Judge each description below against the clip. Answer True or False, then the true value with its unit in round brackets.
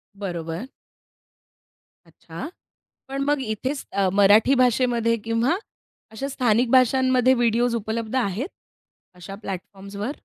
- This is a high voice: True (230 Hz)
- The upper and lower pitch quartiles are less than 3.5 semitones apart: False (4.2 semitones)